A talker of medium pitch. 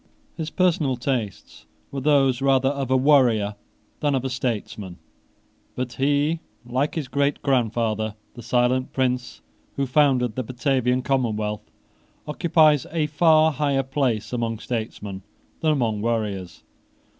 No: low, 130 Hz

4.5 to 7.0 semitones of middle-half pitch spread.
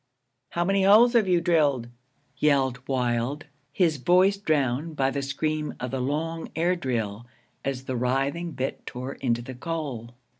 Yes: average, 4.8 semitones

